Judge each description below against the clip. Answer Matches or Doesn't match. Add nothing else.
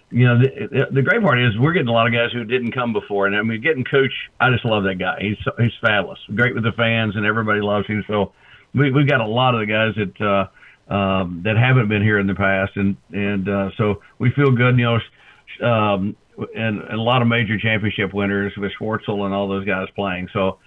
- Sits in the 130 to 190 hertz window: Doesn't match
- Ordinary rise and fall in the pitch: Matches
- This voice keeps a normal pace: Doesn't match